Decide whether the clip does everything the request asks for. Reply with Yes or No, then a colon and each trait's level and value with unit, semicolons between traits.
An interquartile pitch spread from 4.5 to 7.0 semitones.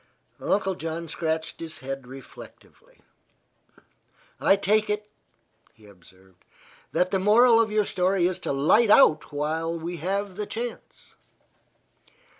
Yes: average, 5.3 semitones